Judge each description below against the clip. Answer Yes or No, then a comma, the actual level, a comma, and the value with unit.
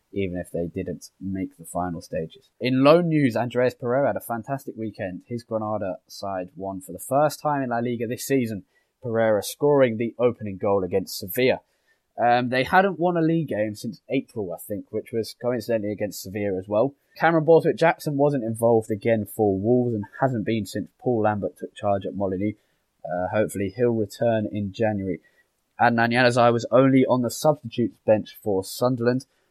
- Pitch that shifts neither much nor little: Yes, average, 3.8 semitones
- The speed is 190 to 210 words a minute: No, average, 180 wpm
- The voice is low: Yes, low, 115 Hz